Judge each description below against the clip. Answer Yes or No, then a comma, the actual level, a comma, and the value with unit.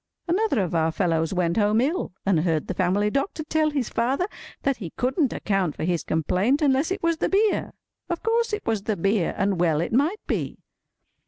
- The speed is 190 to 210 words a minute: Yes, average, 200 wpm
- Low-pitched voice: No, high, 220 Hz